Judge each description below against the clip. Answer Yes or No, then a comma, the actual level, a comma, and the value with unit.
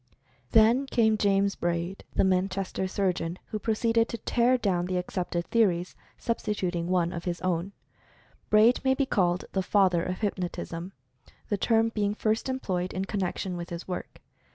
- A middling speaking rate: Yes, average, 160 wpm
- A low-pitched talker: No, high, 190 Hz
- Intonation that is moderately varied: Yes, average, 3.6 semitones